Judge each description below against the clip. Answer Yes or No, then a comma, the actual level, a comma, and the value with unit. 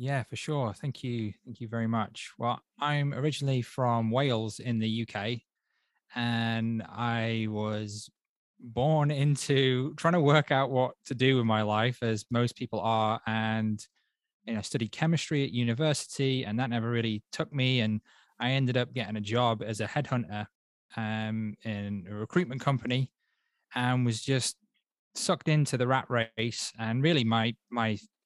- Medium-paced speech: Yes, average, 160 wpm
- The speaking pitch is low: Yes, low, 120 Hz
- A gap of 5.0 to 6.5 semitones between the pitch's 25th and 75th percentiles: No, average, 3.2 semitones